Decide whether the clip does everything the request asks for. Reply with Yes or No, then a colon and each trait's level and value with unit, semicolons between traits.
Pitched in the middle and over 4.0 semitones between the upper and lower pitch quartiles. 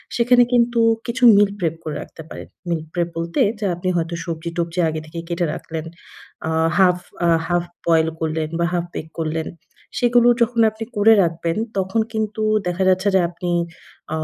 Yes: medium, 175 Hz; average, 4.6 semitones